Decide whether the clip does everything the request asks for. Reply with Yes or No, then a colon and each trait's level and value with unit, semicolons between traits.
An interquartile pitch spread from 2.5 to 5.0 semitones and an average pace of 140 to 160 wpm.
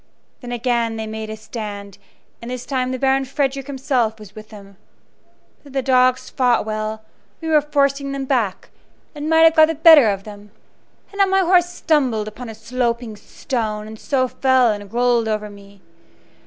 No: average, 4.2 semitones; average, 190 wpm